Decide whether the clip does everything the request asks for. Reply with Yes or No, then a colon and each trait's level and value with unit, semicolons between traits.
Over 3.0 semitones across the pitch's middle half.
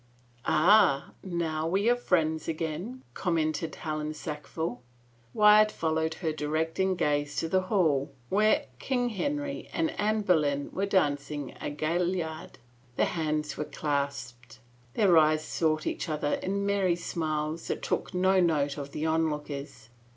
Yes: average, 3.9 semitones